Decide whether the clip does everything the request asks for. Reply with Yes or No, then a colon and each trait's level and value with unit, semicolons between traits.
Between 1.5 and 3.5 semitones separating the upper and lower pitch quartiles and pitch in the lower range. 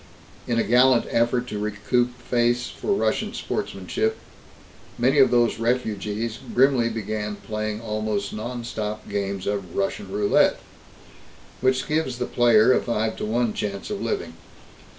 Yes: narrow, 2.6 semitones; low, 115 Hz